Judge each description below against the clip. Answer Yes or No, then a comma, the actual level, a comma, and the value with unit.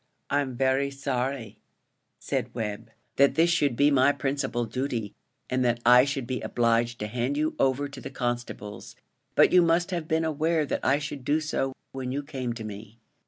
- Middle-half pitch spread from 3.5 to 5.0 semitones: No, average, 3.1 semitones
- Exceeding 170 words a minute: Yes, average, 185 wpm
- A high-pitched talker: No, low, 135 Hz